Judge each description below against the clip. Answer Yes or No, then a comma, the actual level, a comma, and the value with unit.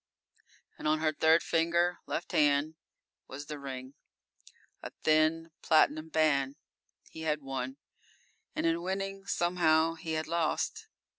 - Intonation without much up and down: Yes, narrow, 2.0 semitones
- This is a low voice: No, medium, 160 Hz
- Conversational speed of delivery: No, slow, 130 wpm